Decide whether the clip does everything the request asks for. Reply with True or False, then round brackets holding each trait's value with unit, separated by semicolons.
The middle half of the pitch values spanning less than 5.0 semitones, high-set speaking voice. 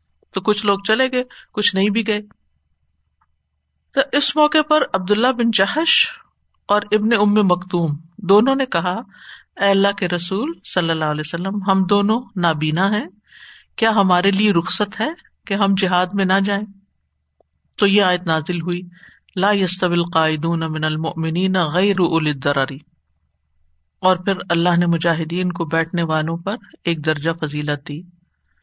False (4.0 semitones; 180 Hz)